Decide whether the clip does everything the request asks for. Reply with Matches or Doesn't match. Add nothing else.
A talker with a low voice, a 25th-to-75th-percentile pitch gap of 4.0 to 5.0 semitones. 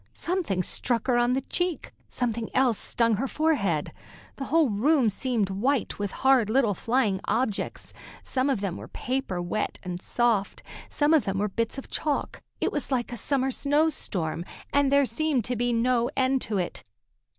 Doesn't match